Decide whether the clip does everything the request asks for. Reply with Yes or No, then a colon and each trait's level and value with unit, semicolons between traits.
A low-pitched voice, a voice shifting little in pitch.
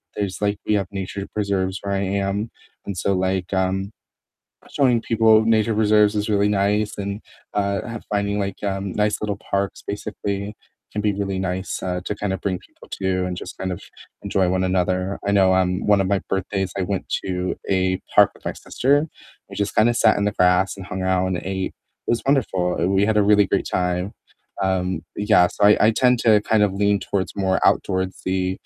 Yes: low, 100 Hz; narrow, 1.8 semitones